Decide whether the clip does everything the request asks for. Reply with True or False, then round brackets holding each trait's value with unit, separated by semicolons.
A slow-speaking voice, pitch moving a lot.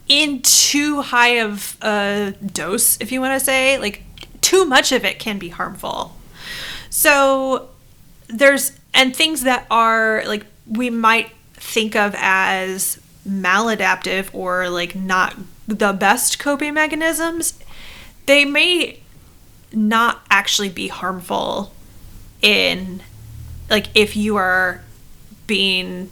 True (115 wpm; 5.8 semitones)